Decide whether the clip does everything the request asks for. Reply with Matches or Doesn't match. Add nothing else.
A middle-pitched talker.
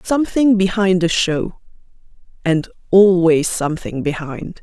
Matches